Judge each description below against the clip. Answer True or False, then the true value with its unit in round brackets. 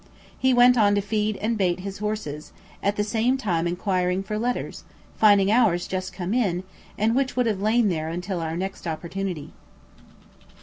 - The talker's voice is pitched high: True (200 Hz)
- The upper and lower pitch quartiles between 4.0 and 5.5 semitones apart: False (3.6 semitones)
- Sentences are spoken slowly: False (175 wpm)